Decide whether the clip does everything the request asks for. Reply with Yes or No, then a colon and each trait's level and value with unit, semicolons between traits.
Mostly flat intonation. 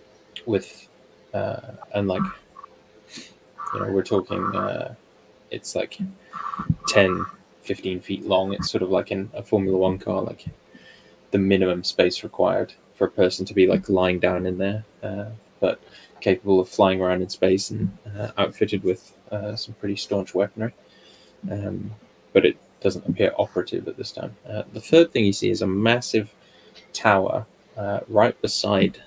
Yes: narrow, 2.3 semitones